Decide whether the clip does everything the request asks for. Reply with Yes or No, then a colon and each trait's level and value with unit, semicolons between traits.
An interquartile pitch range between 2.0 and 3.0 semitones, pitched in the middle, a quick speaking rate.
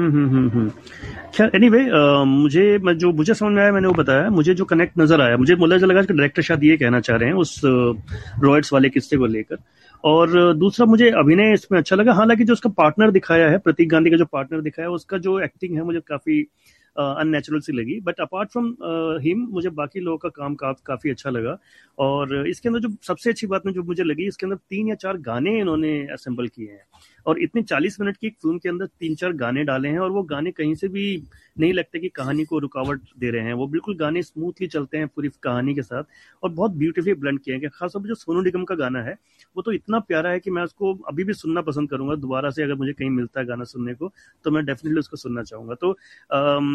No: average, 5.1 semitones; medium, 165 Hz; fast, 235 wpm